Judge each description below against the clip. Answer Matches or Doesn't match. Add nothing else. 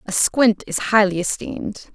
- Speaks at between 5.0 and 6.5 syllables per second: Doesn't match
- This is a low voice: Doesn't match